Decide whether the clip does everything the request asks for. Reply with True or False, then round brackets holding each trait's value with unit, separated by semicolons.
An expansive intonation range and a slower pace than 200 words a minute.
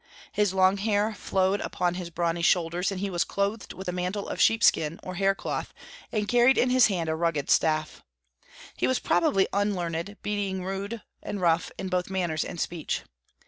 False (3.0 semitones; 185 wpm)